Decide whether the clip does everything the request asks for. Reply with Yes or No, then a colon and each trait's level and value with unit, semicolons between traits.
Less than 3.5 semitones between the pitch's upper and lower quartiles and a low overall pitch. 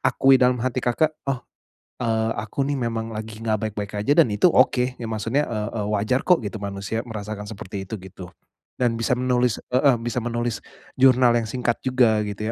Yes: average, 2.8 semitones; low, 115 Hz